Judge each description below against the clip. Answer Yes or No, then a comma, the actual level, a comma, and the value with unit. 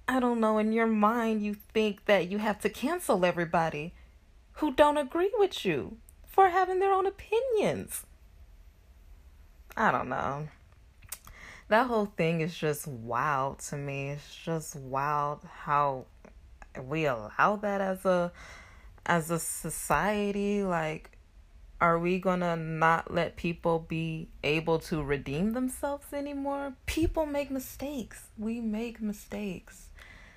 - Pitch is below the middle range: No, medium, 175 Hz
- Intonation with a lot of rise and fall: Yes, wide, 7.7 semitones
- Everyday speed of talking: No, slow, 130 wpm